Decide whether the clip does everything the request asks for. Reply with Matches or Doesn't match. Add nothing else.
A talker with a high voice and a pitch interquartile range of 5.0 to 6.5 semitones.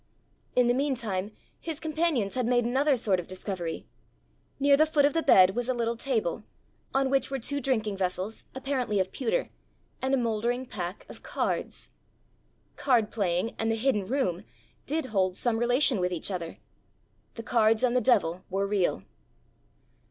Matches